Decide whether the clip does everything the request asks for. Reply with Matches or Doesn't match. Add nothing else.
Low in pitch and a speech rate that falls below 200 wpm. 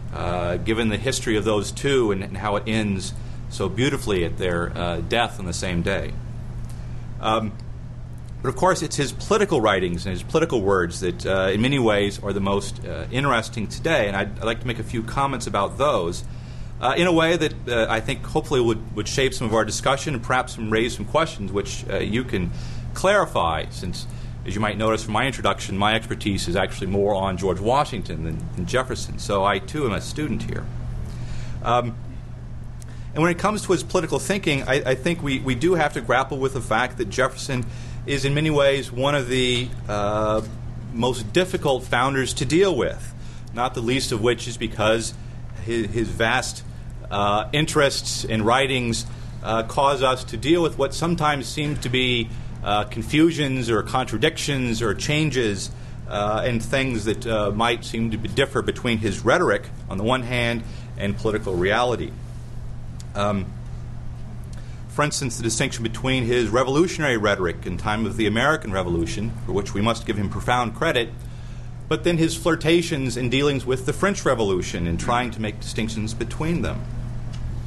Matches